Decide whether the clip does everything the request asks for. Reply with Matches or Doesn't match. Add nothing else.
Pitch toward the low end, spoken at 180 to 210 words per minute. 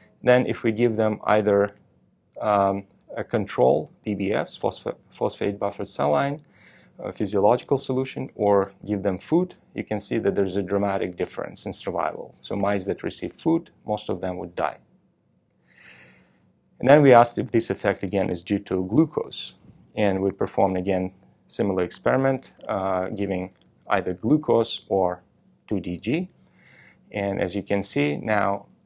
Doesn't match